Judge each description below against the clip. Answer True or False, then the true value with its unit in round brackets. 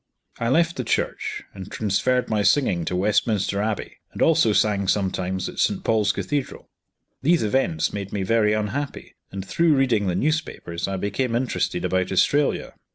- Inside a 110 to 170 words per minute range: True (160 wpm)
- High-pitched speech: False (105 Hz)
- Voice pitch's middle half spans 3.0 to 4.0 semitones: False (5.2 semitones)